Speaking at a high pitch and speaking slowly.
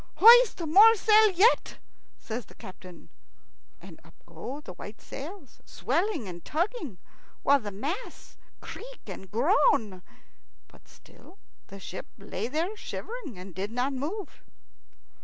Yes: very high, 285 Hz; slow, 130 wpm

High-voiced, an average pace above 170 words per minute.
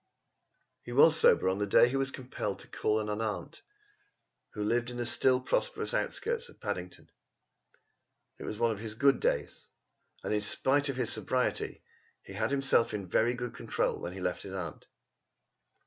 No: low, 115 Hz; average, 180 wpm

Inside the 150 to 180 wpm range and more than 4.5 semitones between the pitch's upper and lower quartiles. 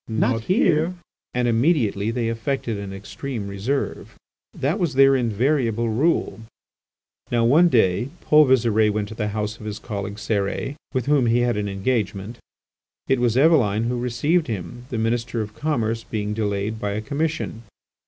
No: average, 160 wpm; average, 4.0 semitones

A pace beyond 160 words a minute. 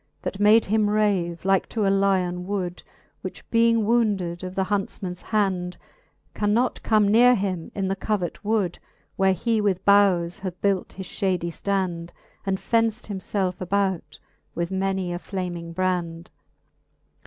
No: average, 150 wpm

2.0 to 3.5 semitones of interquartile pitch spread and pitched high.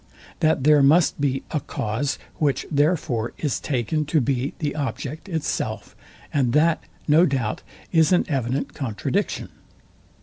No: average, 3.0 semitones; medium, 145 Hz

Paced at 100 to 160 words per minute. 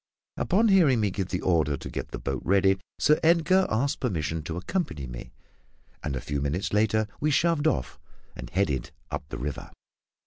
No: average, 180 wpm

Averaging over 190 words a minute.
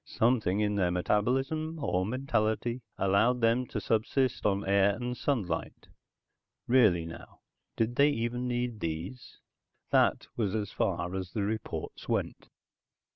No: slow, 135 wpm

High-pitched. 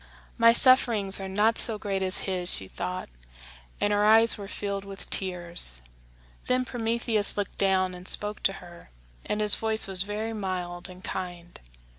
Yes: high, 200 Hz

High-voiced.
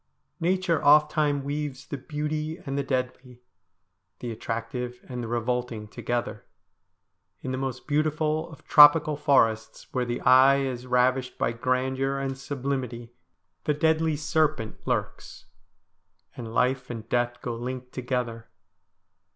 No: low, 130 Hz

